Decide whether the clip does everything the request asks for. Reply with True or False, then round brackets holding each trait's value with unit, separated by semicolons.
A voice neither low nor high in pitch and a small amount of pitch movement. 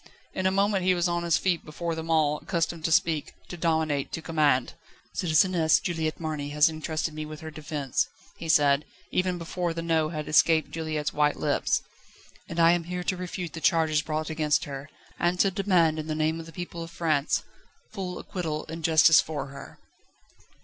True (160 Hz; 2.0 semitones)